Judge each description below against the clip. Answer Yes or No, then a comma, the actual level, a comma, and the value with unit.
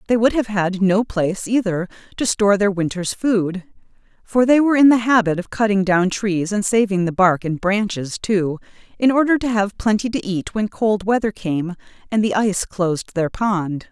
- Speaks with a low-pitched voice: No, high, 205 Hz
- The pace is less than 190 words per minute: No, average, 200 wpm